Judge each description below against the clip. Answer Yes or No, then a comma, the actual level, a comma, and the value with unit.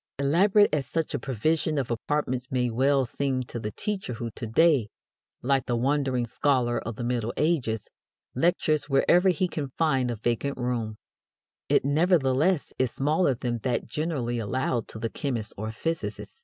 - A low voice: Yes, low, 130 Hz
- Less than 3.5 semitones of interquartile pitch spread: No, average, 4.2 semitones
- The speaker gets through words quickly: No, average, 165 wpm